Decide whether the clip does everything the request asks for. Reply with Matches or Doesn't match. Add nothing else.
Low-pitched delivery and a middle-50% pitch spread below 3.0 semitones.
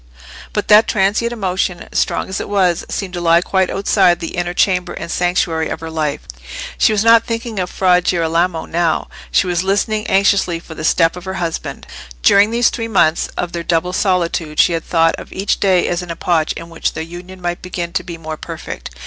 Doesn't match